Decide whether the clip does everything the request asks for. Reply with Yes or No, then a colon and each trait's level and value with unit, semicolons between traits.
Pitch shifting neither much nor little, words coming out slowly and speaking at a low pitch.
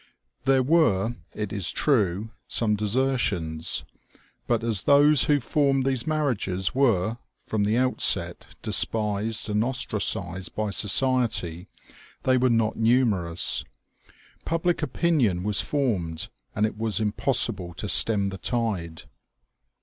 Yes: average, 4.8 semitones; slow, 120 wpm; low, 110 Hz